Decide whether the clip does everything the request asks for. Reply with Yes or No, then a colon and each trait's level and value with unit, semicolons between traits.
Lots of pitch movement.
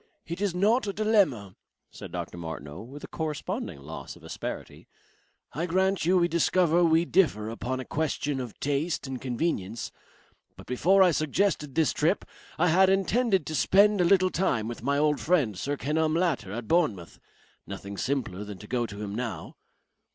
Yes: wide, 7.6 semitones